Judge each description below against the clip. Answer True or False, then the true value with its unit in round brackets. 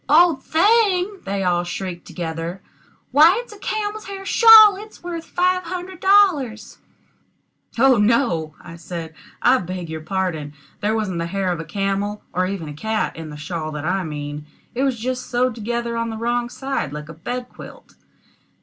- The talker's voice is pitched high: True (220 Hz)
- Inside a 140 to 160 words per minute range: False (175 wpm)